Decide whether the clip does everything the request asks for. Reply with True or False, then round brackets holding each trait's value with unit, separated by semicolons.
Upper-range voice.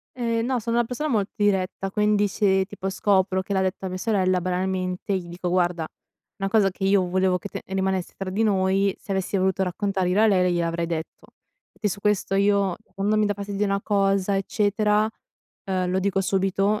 True (195 Hz)